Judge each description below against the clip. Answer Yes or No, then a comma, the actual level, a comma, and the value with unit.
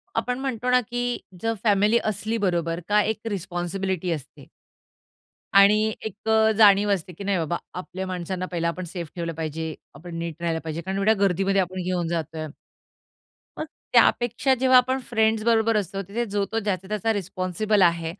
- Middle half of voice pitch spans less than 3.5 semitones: No, average, 4.1 semitones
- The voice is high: Yes, high, 195 Hz